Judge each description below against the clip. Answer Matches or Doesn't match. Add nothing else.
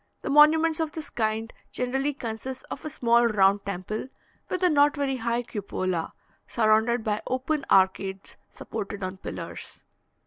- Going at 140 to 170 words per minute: Matches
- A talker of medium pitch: Doesn't match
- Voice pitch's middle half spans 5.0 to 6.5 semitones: Matches